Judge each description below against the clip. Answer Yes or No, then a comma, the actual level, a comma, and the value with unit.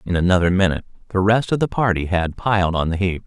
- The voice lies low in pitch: Yes, very low, 95 Hz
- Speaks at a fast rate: Yes, fast, 240 wpm